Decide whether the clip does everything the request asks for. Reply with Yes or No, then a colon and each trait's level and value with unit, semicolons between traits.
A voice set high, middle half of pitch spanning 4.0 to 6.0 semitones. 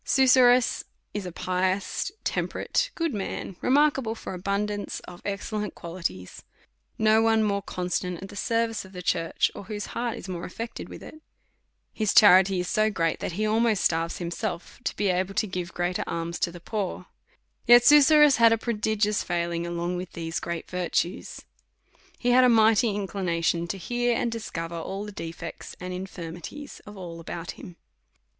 Yes: high, 195 Hz; average, 4.3 semitones